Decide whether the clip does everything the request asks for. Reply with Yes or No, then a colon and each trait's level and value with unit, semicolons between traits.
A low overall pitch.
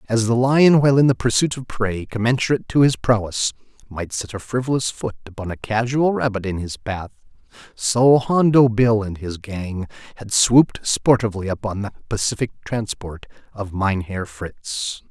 Yes: low, 110 Hz